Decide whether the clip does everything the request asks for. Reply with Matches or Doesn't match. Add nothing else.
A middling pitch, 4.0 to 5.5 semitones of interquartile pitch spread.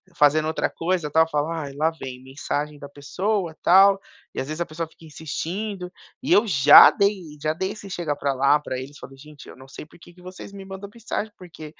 Matches